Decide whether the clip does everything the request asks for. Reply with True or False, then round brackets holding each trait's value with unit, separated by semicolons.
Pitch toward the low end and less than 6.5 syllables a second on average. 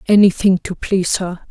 False (190 Hz; 5.2 syllables/s)